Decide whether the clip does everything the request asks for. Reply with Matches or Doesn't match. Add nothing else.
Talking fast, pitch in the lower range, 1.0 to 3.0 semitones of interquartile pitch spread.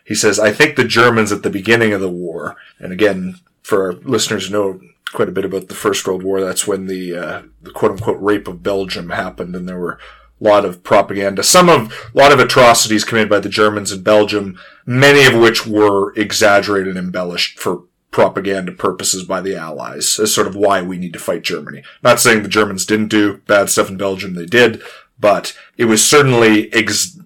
Matches